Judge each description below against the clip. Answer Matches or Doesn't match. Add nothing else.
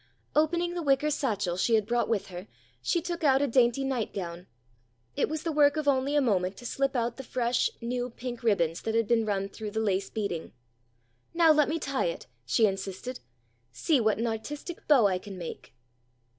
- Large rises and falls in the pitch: Matches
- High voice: Matches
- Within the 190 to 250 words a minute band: Matches